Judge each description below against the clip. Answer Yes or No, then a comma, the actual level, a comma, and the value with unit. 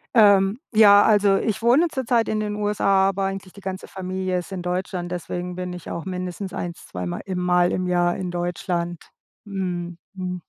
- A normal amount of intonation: No, narrow, 2.2 semitones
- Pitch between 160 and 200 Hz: Yes, medium, 185 Hz